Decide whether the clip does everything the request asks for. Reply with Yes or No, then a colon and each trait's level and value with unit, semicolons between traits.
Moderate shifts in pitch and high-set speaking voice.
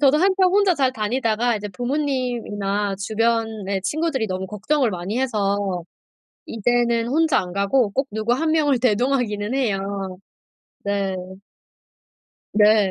Yes: average, 4.6 semitones; high, 230 Hz